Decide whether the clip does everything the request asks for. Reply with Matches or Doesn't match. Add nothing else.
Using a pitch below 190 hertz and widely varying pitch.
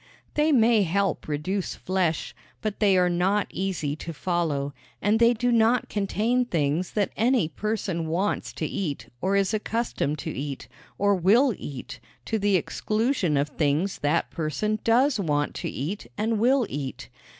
Doesn't match